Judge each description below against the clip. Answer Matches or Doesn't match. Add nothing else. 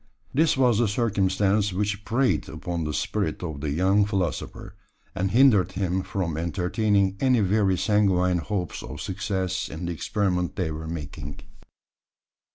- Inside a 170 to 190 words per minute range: Doesn't match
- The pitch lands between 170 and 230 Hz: Doesn't match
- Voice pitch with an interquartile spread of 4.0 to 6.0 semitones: Doesn't match